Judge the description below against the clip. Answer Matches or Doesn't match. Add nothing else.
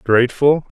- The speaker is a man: Matches